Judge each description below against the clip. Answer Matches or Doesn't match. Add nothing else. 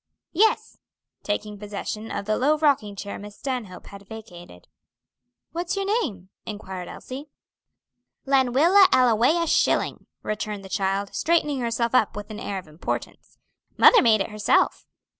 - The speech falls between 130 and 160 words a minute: Matches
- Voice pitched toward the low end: Doesn't match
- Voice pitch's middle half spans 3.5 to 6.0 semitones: Matches